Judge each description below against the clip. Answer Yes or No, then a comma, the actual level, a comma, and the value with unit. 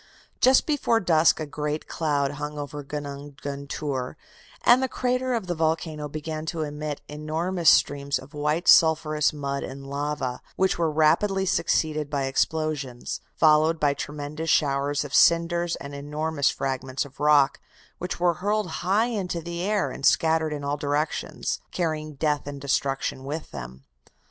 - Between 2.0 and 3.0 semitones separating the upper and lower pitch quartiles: Yes, average, 2.7 semitones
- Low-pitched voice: No, medium, 150 Hz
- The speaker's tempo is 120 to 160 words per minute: Yes, average, 155 wpm